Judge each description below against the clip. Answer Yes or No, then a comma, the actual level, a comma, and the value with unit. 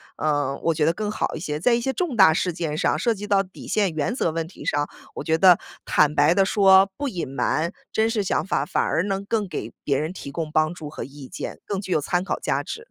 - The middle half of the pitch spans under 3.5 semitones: No, average, 4.7 semitones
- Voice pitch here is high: No, medium, 175 Hz